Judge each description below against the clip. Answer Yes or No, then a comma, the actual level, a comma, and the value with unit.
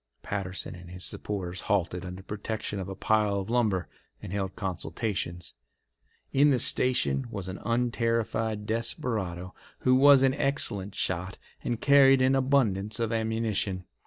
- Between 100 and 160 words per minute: Yes, average, 140 wpm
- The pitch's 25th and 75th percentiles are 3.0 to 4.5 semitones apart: Yes, average, 4.1 semitones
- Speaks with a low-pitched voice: Yes, low, 105 Hz